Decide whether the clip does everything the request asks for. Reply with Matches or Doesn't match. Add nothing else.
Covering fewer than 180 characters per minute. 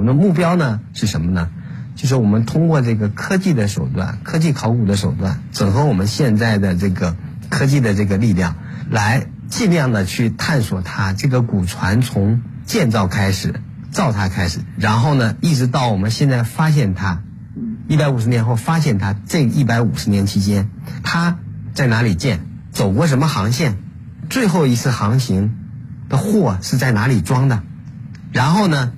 Doesn't match